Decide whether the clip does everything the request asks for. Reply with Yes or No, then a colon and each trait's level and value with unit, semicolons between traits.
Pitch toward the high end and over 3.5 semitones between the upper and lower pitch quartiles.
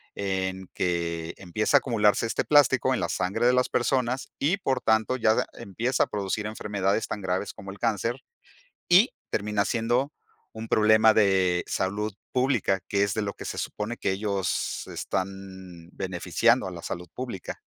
No: low, 105 Hz; average, 3.9 semitones